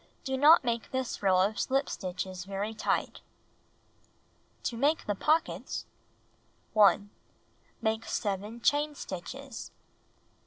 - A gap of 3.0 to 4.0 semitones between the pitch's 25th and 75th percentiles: No, wide, 5.5 semitones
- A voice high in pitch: Yes, high, 220 Hz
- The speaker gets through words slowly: Yes, slow, 110 wpm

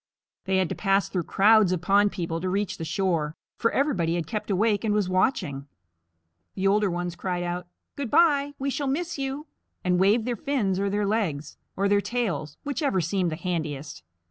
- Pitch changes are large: No, average, 4.3 semitones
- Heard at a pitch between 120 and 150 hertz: No, high, 195 Hz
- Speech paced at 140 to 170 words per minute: No, average, 195 wpm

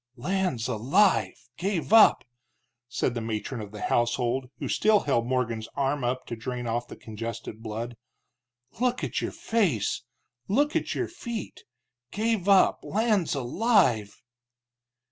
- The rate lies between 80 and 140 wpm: Yes, slow, 135 wpm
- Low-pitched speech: Yes, low, 130 Hz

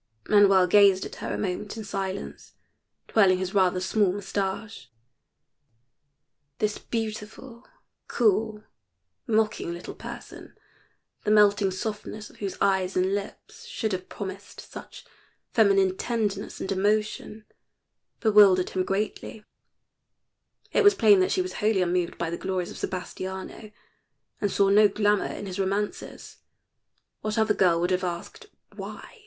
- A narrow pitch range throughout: Yes, narrow, 2.2 semitones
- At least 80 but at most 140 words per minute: Yes, slow, 135 wpm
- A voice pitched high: Yes, high, 200 Hz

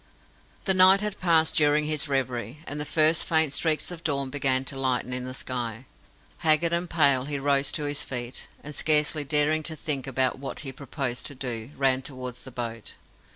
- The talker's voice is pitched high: No, medium, 140 Hz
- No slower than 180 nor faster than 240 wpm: Yes, average, 195 wpm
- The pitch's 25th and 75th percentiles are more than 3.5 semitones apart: No, average, 3.1 semitones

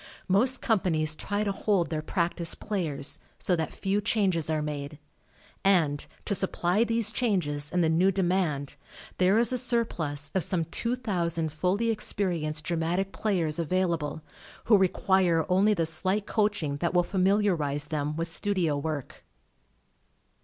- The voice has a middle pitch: Yes, medium, 180 Hz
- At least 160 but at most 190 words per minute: No, average, 145 wpm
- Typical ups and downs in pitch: Yes, average, 4.3 semitones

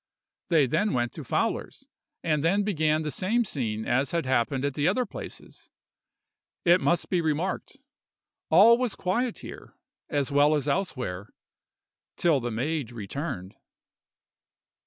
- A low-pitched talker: No, medium, 150 Hz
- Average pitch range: No, wide, 5.9 semitones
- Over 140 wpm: No, slow, 135 wpm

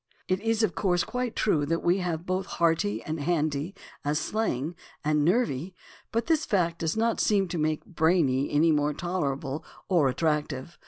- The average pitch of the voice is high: No, medium, 165 Hz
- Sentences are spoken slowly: No, average, 170 wpm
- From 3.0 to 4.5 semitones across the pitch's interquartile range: Yes, average, 4.2 semitones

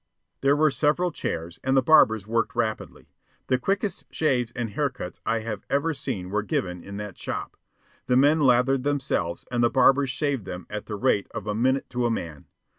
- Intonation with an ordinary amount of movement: Yes, average, 4.8 semitones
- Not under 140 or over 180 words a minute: No, average, 195 wpm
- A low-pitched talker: Yes, low, 125 Hz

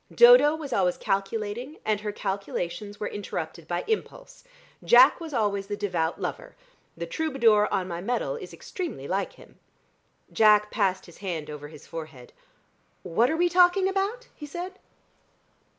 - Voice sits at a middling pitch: No, high, 210 Hz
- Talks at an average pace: Yes, average, 150 wpm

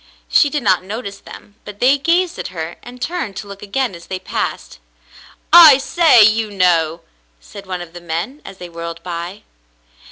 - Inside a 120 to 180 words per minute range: No, average, 190 wpm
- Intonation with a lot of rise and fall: Yes, wide, 6.6 semitones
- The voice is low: No, high, 200 Hz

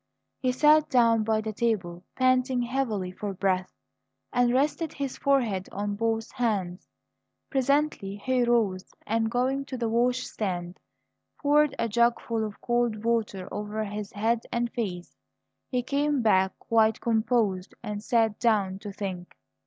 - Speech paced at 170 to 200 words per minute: No, average, 145 wpm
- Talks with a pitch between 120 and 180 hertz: No, high, 225 Hz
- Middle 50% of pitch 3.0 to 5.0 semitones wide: Yes, average, 3.5 semitones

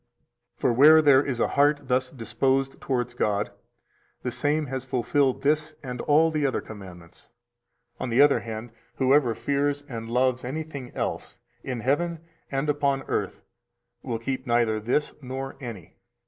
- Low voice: Yes, low, 130 Hz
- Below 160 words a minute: Yes, average, 150 wpm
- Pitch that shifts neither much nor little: Yes, average, 3.1 semitones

